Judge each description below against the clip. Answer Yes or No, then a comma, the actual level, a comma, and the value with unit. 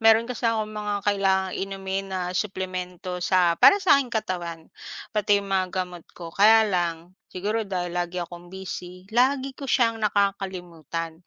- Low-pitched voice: No, high, 190 Hz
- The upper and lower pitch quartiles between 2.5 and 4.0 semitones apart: Yes, average, 3.2 semitones